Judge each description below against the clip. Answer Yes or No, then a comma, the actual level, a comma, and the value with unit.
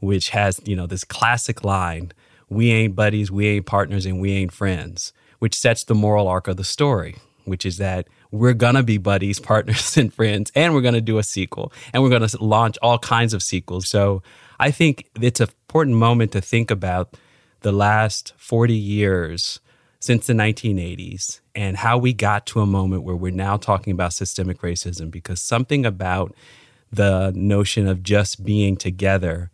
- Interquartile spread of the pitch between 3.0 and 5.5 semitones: Yes, average, 3.6 semitones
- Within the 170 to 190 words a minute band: Yes, average, 185 wpm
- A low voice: Yes, low, 105 Hz